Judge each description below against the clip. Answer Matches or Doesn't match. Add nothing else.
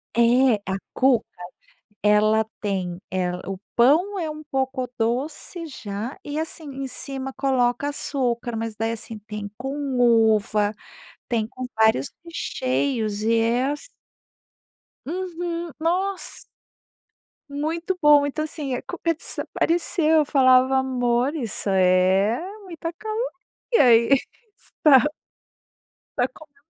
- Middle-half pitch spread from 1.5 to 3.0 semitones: Doesn't match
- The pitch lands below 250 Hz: Doesn't match